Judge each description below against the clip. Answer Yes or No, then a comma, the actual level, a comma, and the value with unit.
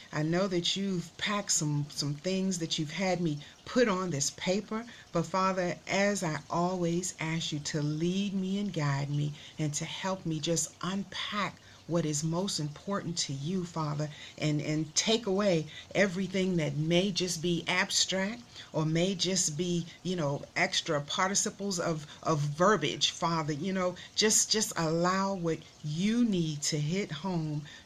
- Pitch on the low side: No, medium, 170 Hz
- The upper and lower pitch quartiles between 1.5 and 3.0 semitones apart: No, average, 3.5 semitones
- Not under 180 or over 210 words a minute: No, average, 160 wpm